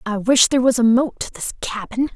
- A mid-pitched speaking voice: No, high, 240 Hz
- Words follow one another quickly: Yes, fast, 250 wpm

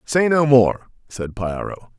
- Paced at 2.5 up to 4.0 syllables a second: Yes, 3.7 syllables/s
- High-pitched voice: No, low, 120 Hz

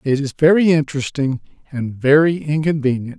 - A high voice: No, medium, 145 Hz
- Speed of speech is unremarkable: No, slow, 130 wpm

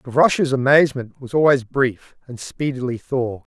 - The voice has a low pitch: Yes, low, 130 Hz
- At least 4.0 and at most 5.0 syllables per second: No, 5.4 syllables/s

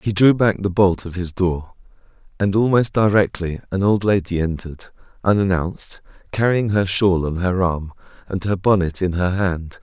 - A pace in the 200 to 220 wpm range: No, average, 170 wpm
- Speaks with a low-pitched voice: Yes, very low, 95 Hz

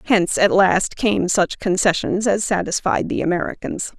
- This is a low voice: No, high, 190 Hz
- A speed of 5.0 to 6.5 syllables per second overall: No, 4.7 syllables/s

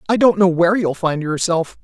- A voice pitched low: No, medium, 180 Hz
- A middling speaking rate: No, fast, 230 wpm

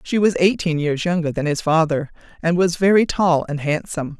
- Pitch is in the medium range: Yes, medium, 165 Hz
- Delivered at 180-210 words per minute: Yes, average, 200 wpm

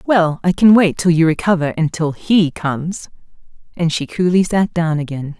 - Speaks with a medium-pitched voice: Yes, medium, 170 Hz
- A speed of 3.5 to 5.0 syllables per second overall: Yes, 4.8 syllables/s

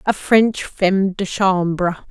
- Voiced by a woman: Yes, female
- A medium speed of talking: Yes, average, 145 wpm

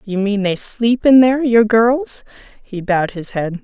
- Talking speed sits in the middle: Yes, average, 180 wpm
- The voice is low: No, high, 215 Hz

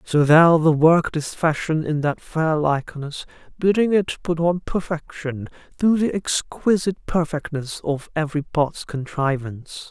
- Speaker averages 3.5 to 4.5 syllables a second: Yes, 4.3 syllables/s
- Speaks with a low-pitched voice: No, medium, 160 Hz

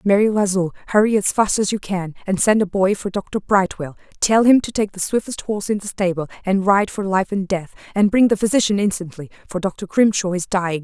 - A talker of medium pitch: No, high, 195 Hz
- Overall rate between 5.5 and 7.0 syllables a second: Yes, 5.6 syllables/s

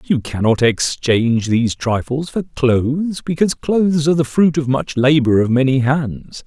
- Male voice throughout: Yes, male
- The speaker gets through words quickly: No, average, 165 wpm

